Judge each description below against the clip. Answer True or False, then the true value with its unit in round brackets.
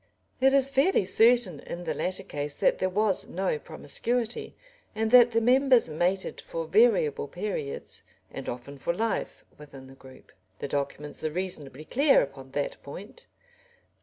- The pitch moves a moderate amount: False (8.0 semitones)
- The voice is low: False (185 Hz)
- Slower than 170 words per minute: True (160 wpm)